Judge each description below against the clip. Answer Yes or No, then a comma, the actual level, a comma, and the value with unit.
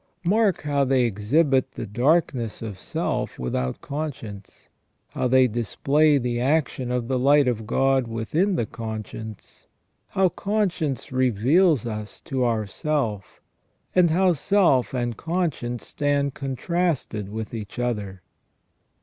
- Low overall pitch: Yes, low, 130 Hz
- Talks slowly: Yes, slow, 125 wpm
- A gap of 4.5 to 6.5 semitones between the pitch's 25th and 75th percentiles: Yes, average, 5.3 semitones